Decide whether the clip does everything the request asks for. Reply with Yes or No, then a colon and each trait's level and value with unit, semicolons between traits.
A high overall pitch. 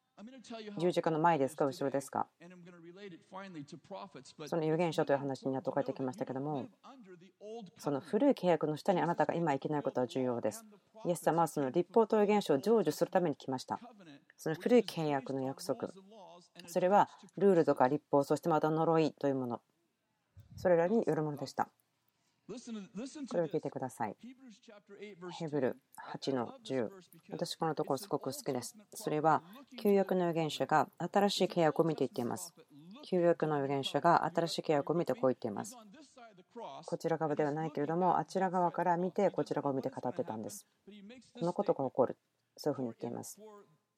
No: medium, 165 Hz